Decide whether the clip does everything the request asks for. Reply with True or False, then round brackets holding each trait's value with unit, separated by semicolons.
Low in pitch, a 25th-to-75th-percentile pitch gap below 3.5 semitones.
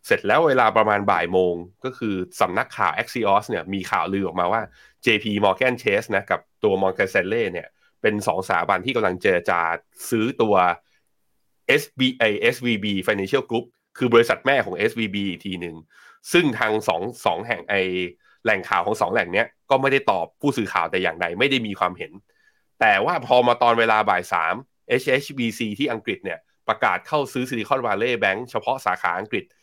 False (110 Hz; 5.0 semitones)